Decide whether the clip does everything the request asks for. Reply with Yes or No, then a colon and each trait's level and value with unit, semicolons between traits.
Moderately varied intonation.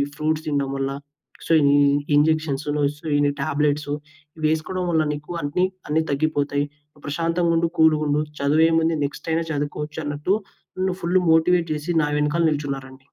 No: narrow, 2.0 semitones